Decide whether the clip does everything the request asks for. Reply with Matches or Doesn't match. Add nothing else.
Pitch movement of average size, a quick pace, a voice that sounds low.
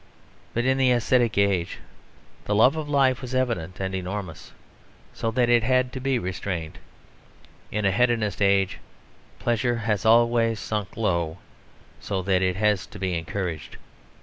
Doesn't match